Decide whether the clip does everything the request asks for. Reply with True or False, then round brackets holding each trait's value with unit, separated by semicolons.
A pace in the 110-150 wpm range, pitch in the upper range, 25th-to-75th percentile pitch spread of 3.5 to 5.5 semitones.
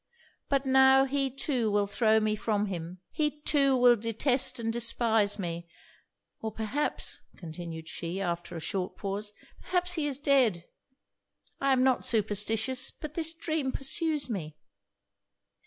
True (140 wpm; 230 Hz; 5.2 semitones)